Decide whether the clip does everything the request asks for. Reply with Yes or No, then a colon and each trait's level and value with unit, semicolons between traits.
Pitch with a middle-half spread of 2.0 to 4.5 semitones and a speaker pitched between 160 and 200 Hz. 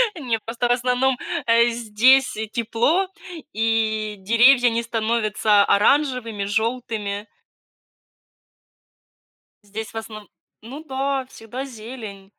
No: average, 2.7 semitones; high, 230 Hz